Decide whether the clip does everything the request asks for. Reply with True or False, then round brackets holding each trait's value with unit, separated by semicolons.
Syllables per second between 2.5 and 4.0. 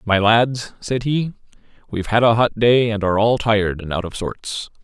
False (5.1 syllables/s)